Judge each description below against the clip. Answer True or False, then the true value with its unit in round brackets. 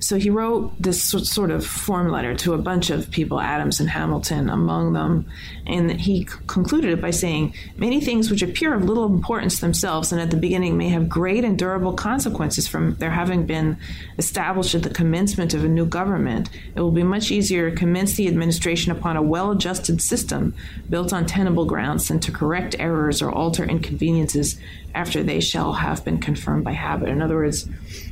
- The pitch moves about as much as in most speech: True (3.0 semitones)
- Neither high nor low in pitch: True (170 Hz)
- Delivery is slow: False (195 wpm)